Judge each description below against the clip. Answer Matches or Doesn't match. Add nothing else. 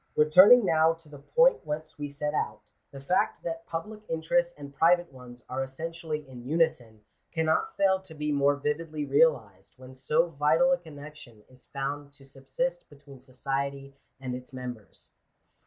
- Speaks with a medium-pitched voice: Matches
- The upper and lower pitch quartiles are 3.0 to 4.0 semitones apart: Matches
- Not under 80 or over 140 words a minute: Doesn't match